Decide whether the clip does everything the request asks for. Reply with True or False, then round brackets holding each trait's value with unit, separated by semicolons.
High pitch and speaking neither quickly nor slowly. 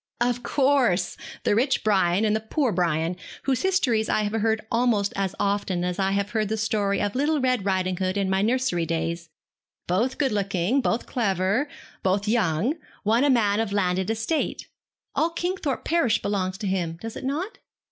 True (210 Hz; 175 wpm)